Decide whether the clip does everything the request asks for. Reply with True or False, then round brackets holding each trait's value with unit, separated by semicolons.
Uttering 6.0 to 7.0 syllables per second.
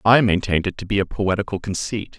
True (6.2 syllables/s)